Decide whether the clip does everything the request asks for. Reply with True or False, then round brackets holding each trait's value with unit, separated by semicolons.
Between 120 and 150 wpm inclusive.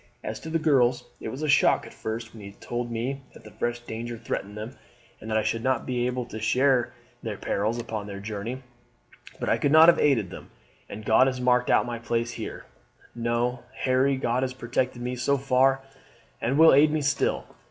False (205 wpm)